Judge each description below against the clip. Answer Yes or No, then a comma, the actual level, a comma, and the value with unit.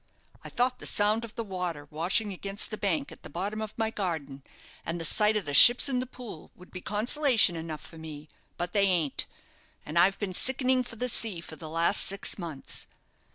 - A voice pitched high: Yes, high, 195 Hz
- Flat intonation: No, average, 5.1 semitones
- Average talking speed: No, fast, 210 wpm